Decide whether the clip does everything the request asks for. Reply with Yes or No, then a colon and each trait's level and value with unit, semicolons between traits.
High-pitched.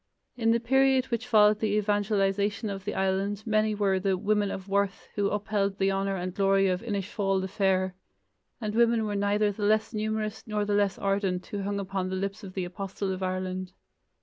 Yes: high, 200 Hz